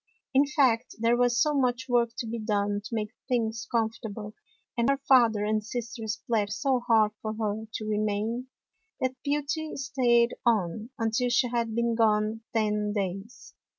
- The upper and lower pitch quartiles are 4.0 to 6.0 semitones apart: No, narrow, 2.5 semitones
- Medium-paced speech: Yes, average, 160 wpm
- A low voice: No, high, 230 Hz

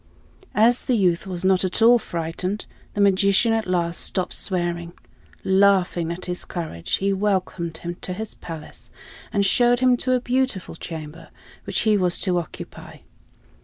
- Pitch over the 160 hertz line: Yes, medium, 185 Hz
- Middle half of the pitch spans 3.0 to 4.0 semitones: Yes, average, 3.5 semitones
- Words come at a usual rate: Yes, average, 160 wpm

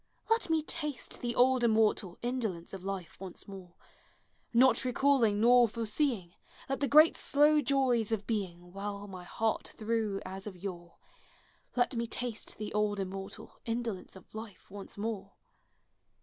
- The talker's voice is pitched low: No, high, 220 Hz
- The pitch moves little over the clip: No, average, 4.0 semitones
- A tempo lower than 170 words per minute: Yes, average, 150 wpm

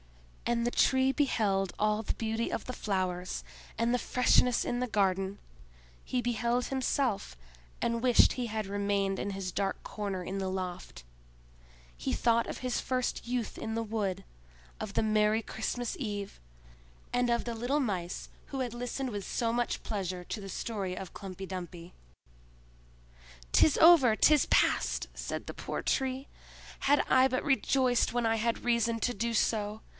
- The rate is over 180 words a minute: No, average, 160 wpm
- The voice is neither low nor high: No, high, 225 Hz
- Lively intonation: No, average, 3.8 semitones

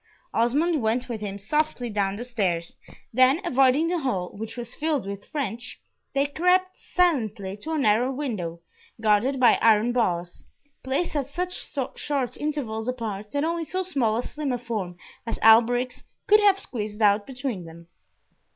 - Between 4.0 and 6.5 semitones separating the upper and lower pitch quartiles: Yes, wide, 5.5 semitones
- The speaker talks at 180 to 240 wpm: No, average, 160 wpm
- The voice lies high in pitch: Yes, high, 245 Hz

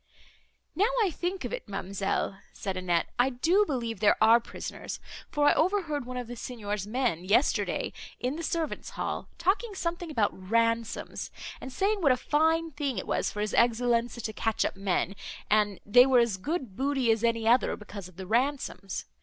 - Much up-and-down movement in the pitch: Yes, wide, 6.2 semitones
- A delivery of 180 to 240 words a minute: Yes, average, 185 wpm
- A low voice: No, high, 240 Hz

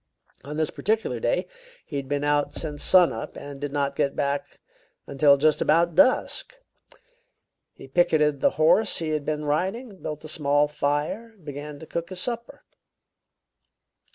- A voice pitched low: No, medium, 150 Hz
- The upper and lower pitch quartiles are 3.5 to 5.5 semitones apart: No, average, 3.0 semitones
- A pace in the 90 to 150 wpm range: No, average, 165 wpm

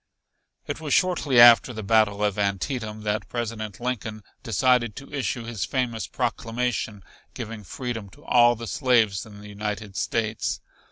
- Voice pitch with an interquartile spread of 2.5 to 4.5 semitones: Yes, average, 2.9 semitones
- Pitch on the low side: Yes, low, 115 Hz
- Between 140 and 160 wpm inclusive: Yes, average, 150 wpm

